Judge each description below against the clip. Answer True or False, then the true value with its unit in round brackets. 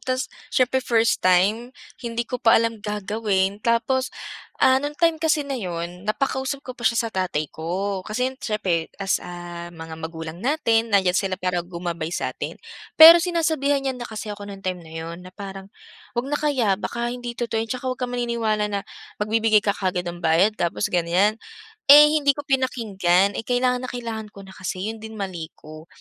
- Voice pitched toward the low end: False (215 Hz)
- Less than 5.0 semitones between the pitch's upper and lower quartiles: False (5.3 semitones)